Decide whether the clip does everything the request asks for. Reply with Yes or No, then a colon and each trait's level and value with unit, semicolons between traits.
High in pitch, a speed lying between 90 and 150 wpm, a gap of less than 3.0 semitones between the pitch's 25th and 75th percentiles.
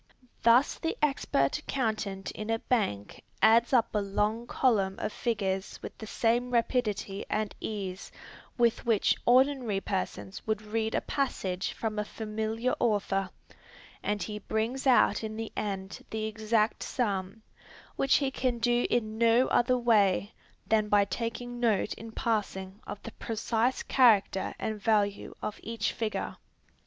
Yes: high, 220 Hz; average, 145 wpm; narrow, 2.6 semitones